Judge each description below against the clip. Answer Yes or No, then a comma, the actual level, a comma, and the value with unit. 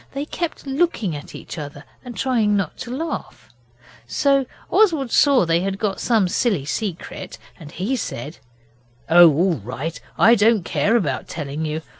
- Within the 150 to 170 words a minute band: Yes, average, 160 wpm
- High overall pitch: Yes, high, 195 Hz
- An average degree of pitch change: No, wide, 8.0 semitones